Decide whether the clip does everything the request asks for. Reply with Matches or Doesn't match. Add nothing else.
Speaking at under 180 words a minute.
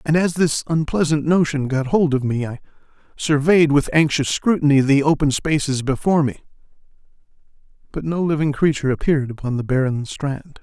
Matches